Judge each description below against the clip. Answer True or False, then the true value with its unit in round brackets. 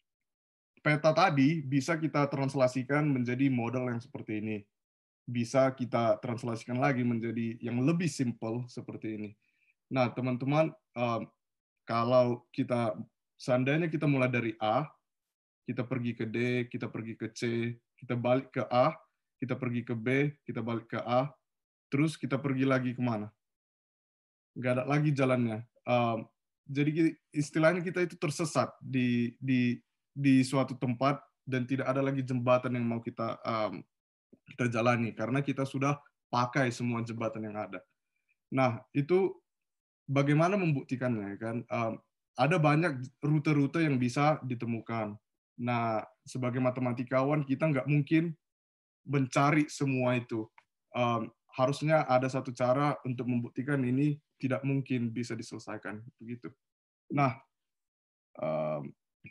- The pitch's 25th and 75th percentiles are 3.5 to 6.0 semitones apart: False (3.0 semitones)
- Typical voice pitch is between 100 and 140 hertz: True (125 Hz)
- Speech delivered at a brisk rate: False (125 wpm)